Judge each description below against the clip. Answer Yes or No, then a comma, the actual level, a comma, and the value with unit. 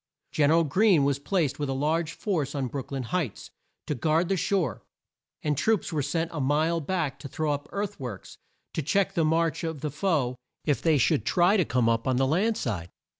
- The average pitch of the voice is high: No, medium, 155 Hz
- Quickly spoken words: Yes, fast, 220 wpm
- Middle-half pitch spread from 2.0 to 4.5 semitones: Yes, average, 3.8 semitones